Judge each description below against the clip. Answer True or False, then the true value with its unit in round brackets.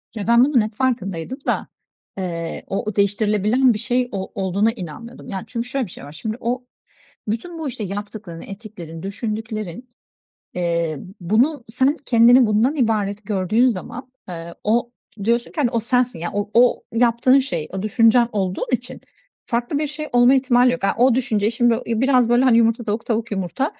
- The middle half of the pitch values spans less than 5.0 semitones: True (3.8 semitones)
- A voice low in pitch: False (230 Hz)